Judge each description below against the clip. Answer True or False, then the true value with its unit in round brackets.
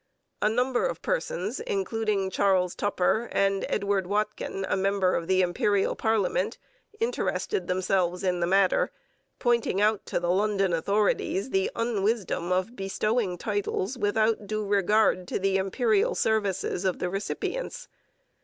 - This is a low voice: False (200 Hz)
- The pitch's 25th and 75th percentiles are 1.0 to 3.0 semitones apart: True (2.7 semitones)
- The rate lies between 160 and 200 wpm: False (135 wpm)